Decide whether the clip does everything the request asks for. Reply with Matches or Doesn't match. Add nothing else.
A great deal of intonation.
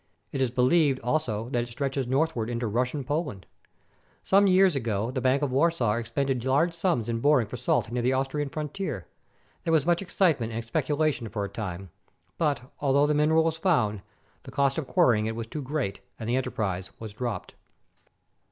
Doesn't match